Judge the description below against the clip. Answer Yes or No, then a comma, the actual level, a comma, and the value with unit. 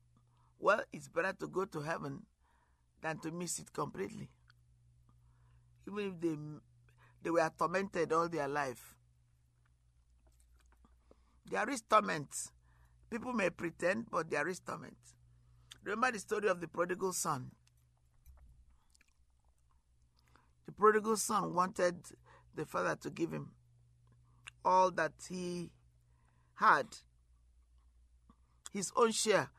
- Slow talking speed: Yes, slow, 110 wpm